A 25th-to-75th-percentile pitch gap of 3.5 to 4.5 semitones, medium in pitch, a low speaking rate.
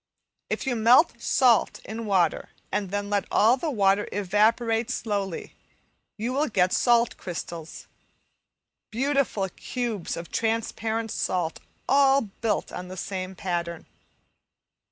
No: average, 3.8 semitones; high, 215 Hz; slow, 120 wpm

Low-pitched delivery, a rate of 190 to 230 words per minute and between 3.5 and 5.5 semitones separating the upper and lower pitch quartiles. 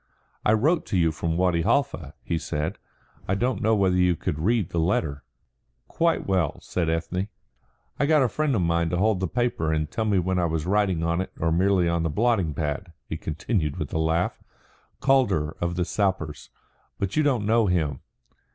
Yes: very low, 90 Hz; average, 195 wpm; average, 4.6 semitones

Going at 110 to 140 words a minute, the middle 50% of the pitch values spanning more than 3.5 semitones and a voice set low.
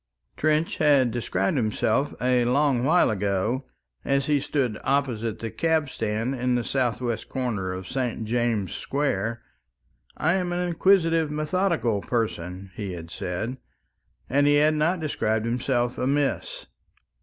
Yes: slow, 135 wpm; average, 4.8 semitones; low, 125 Hz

